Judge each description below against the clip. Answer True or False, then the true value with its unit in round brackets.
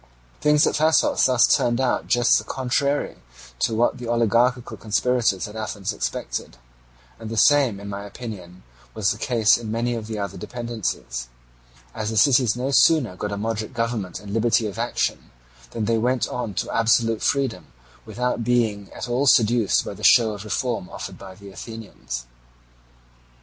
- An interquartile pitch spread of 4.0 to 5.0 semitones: False (2.9 semitones)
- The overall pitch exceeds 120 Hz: False (115 Hz)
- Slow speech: False (170 wpm)